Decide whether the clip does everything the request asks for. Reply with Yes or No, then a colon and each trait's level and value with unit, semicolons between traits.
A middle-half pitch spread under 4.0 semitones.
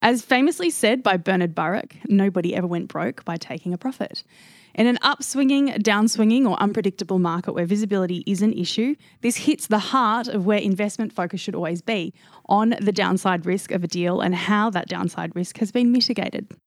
No: average, 4.3 semitones